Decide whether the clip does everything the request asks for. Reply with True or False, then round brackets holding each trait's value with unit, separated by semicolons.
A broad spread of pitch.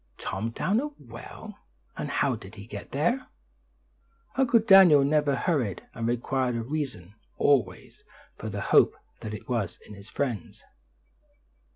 True (6.1 semitones)